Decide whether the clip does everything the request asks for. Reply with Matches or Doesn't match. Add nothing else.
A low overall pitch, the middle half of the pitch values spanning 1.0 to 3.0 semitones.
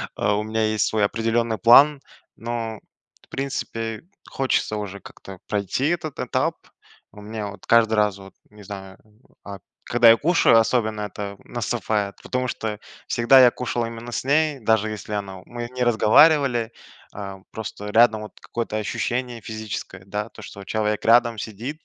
Matches